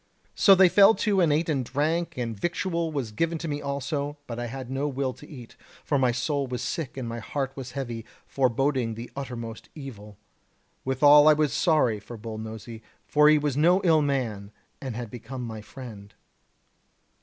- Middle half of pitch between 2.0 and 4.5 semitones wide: Yes, average, 4.1 semitones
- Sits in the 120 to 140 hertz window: Yes, low, 135 Hz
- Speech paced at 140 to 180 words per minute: No, average, 190 wpm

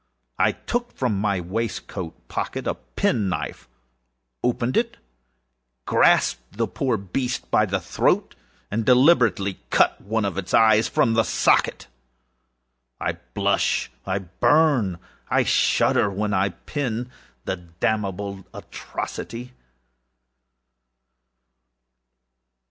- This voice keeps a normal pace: No, slow, 105 wpm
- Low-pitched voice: Yes, low, 105 Hz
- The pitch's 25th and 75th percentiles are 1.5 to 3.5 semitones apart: No, average, 4.2 semitones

